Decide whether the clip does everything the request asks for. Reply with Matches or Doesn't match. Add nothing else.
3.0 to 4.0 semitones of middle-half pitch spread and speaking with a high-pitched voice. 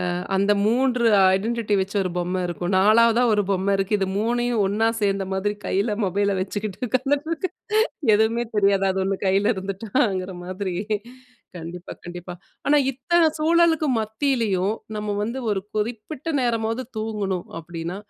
Matches